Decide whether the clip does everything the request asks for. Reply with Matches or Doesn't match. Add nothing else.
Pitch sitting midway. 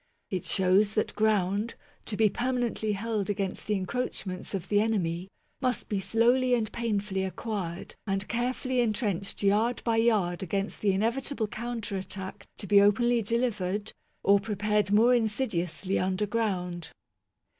Doesn't match